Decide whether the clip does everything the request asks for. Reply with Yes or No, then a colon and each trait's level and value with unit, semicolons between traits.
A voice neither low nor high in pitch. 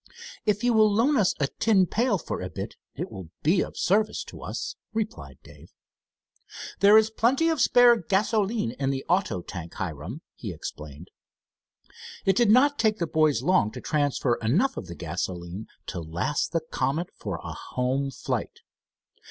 Yes: medium, 165 Hz